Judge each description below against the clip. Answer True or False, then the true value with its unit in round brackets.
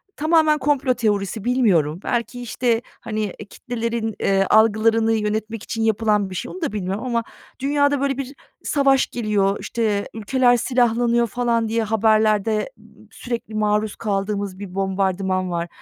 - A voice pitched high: True (220 Hz)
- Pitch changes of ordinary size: True (3.2 semitones)